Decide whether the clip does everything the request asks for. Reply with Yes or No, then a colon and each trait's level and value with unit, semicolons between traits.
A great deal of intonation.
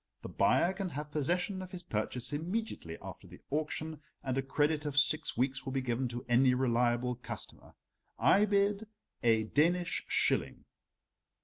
Yes: wide, 5.9 semitones